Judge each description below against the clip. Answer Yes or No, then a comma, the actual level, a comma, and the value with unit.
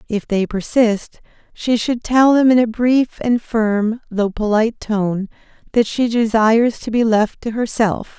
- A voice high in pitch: Yes, high, 225 Hz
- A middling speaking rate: Yes, average, 170 wpm